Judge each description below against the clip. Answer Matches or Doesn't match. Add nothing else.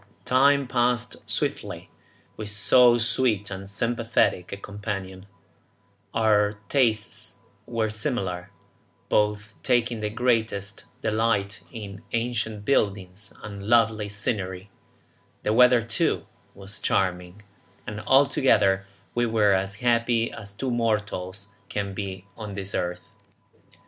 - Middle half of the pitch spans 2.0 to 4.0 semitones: Matches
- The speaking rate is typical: Doesn't match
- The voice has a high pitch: Doesn't match